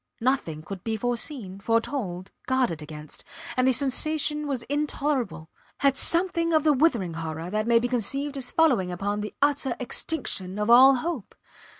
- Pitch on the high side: Yes, high, 245 Hz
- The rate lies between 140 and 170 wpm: Yes, average, 160 wpm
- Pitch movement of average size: No, wide, 6.5 semitones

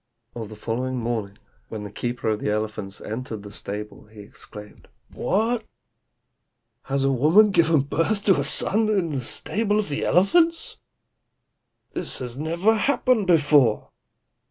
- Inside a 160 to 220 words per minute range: No, average, 140 wpm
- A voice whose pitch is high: No, medium, 140 Hz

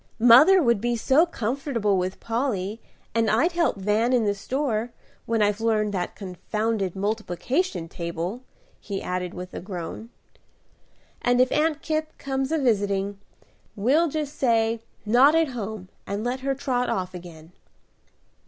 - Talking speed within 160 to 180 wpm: No, average, 145 wpm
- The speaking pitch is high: Yes, high, 225 Hz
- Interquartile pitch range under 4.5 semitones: No, average, 5.2 semitones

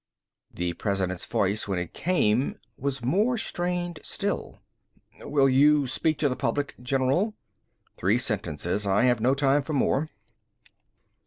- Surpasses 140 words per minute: No, slow, 135 wpm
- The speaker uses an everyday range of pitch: No, wide, 6.2 semitones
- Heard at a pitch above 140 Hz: No, low, 130 Hz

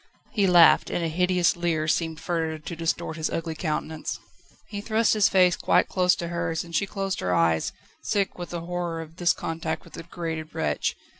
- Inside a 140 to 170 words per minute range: No, average, 200 wpm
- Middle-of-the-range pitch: Yes, medium, 170 Hz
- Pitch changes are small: Yes, narrow, 2.0 semitones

